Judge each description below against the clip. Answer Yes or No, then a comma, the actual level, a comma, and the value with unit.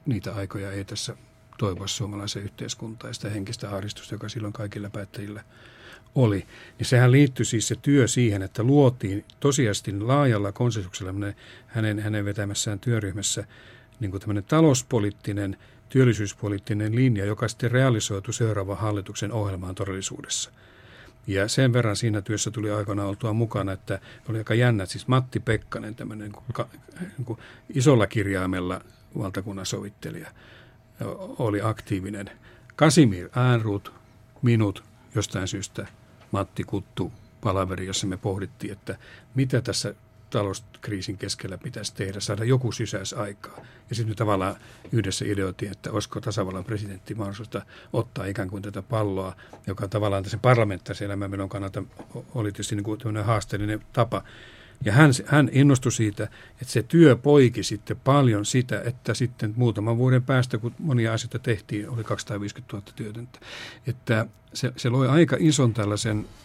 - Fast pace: No, average, 140 wpm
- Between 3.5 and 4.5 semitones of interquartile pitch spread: No, average, 3.1 semitones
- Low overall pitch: Yes, low, 110 Hz